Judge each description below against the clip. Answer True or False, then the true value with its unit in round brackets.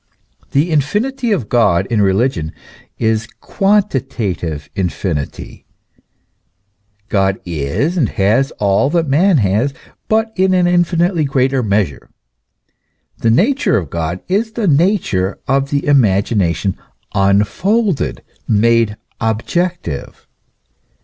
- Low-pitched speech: True (125 Hz)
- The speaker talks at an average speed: False (105 wpm)